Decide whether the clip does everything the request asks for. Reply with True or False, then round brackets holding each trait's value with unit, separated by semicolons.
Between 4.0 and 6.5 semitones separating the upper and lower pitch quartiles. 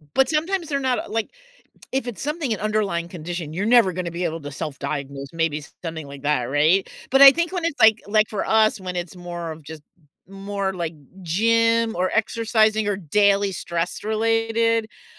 True (5.3 semitones)